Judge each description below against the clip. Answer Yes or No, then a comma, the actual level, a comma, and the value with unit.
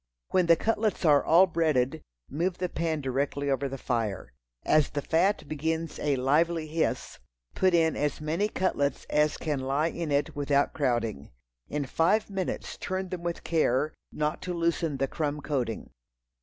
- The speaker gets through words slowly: No, average, 165 wpm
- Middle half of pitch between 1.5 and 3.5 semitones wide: Yes, average, 3.1 semitones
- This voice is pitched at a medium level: Yes, medium, 155 Hz